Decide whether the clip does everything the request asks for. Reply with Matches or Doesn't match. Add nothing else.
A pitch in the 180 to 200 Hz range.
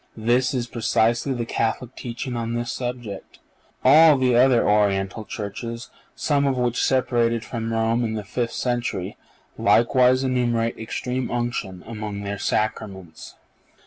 Doesn't match